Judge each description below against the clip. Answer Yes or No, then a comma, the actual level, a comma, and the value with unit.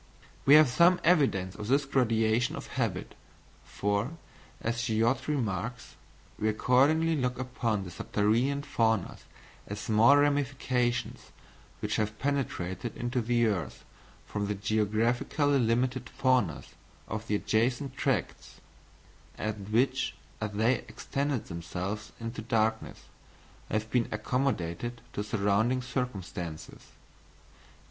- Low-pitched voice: Yes, low, 115 Hz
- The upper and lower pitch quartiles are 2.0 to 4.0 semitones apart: Yes, average, 3.5 semitones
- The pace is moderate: No, slow, 110 wpm